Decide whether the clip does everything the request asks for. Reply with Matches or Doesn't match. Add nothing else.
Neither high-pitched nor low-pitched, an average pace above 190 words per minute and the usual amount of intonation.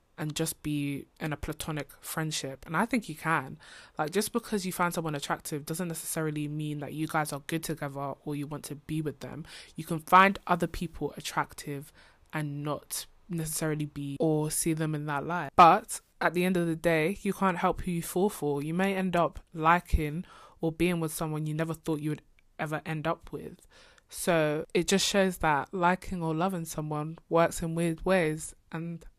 Doesn't match